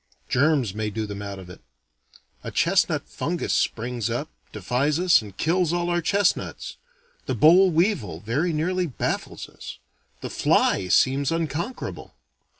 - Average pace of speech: Yes, average, 145 wpm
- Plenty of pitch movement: Yes, wide, 8.1 semitones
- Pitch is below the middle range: No, medium, 145 Hz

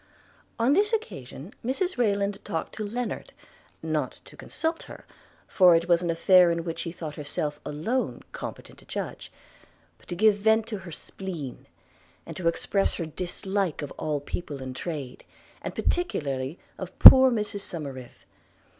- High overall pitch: No, medium, 180 Hz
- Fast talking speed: No, average, 165 wpm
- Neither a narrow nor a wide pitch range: No, wide, 6.1 semitones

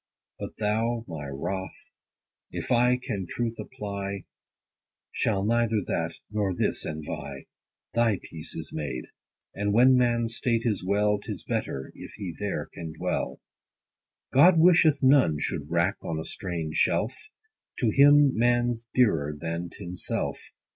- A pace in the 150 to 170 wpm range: No, average, 140 wpm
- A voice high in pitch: No, low, 105 Hz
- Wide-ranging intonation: Yes, wide, 5.9 semitones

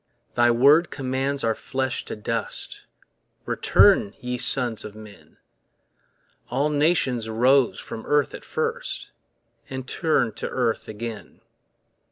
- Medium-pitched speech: No, low, 125 Hz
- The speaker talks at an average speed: No, slow, 120 wpm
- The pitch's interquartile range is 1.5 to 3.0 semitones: No, average, 3.8 semitones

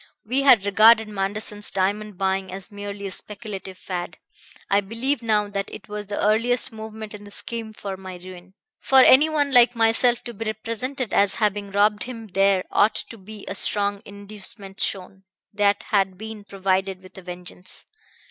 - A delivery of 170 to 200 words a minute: Yes, average, 175 wpm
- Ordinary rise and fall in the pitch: No, narrow, 2.3 semitones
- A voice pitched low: No, high, 205 Hz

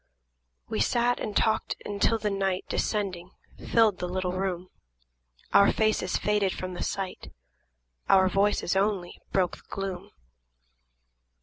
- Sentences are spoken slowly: Yes, slow, 130 wpm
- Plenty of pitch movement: No, narrow, 2.4 semitones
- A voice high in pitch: Yes, high, 195 Hz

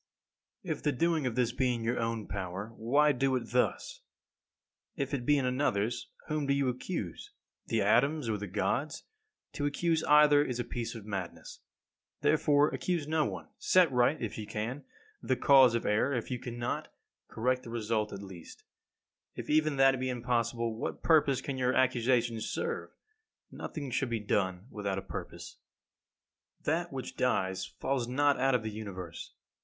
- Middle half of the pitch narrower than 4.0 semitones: No, average, 4.3 semitones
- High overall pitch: No, low, 125 Hz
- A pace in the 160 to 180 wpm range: Yes, average, 175 wpm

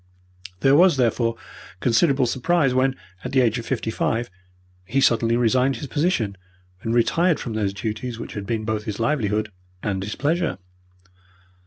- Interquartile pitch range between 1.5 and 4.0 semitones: Yes, average, 3.7 semitones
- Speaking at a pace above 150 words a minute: Yes, average, 160 wpm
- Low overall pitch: Yes, low, 120 Hz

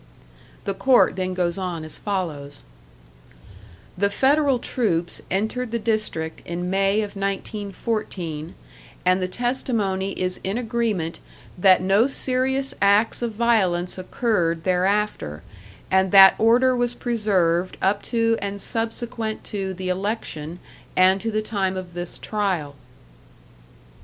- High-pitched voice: Yes, high, 195 Hz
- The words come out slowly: Yes, slow, 125 wpm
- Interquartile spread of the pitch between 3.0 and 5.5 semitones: Yes, average, 3.8 semitones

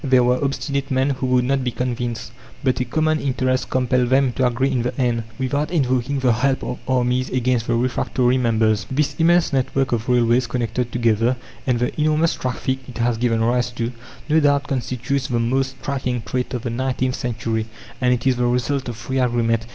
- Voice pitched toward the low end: Yes, low, 125 Hz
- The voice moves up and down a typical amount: No, narrow, 1.7 semitones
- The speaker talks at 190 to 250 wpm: Yes, average, 200 wpm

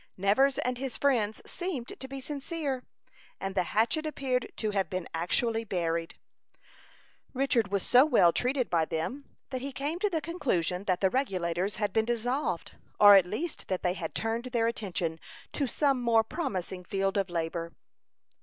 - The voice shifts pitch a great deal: Yes, wide, 6.4 semitones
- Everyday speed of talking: Yes, average, 170 wpm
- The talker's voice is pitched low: No, high, 225 Hz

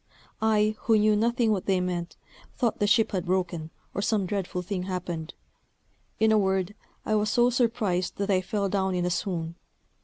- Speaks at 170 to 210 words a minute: Yes, average, 185 wpm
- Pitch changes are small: No, average, 3.0 semitones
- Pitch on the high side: Yes, high, 195 Hz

